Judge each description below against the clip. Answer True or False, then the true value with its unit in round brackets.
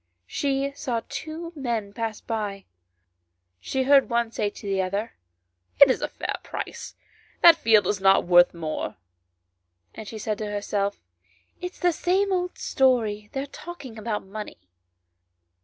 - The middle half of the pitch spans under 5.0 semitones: False (5.4 semitones)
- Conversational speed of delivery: True (155 wpm)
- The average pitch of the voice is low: False (225 Hz)